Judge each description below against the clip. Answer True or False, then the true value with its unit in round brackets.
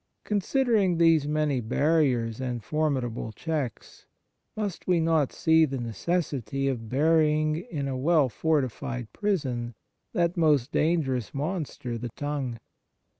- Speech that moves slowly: True (125 wpm)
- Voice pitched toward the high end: False (150 Hz)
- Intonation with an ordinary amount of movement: True (4.4 semitones)